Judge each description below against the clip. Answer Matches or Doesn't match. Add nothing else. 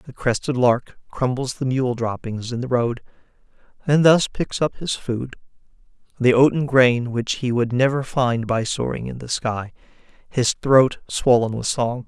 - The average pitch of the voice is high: Doesn't match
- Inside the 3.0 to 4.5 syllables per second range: Matches